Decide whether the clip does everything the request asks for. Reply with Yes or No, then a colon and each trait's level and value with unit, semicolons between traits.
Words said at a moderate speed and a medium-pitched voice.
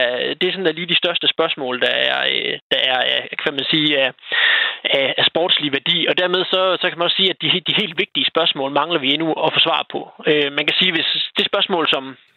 No: fast, 230 wpm; medium, 165 Hz